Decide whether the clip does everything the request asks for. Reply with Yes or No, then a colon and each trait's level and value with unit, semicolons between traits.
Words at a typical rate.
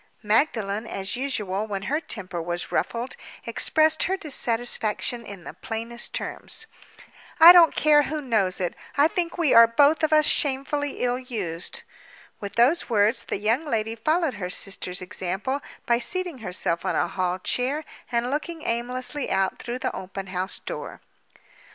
Yes: average, 155 wpm